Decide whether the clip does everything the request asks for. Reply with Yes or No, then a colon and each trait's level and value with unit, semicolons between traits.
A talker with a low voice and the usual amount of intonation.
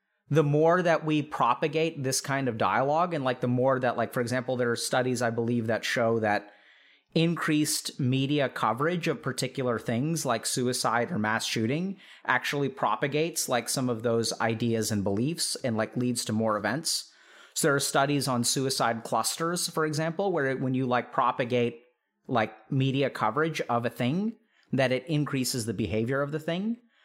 Yes: low, 130 Hz; average, 4.4 semitones